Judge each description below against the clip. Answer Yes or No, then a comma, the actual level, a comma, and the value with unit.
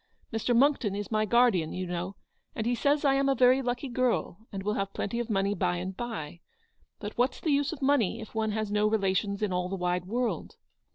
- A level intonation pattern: No, average, 4.2 semitones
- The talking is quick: Yes, fast, 225 wpm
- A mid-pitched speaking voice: No, high, 215 Hz